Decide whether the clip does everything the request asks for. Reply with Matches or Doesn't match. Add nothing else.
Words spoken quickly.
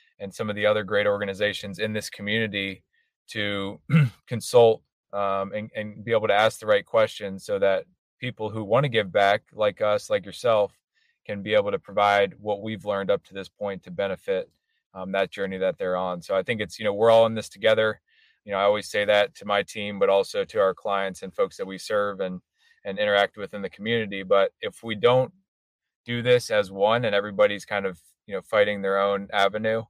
Matches